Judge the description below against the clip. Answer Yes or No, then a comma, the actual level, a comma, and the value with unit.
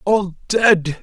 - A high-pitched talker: Yes, high, 195 Hz